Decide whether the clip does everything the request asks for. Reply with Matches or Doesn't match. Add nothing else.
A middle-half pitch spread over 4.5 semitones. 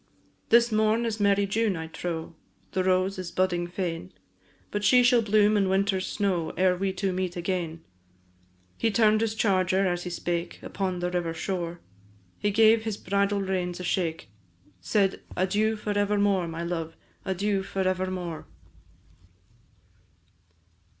Doesn't match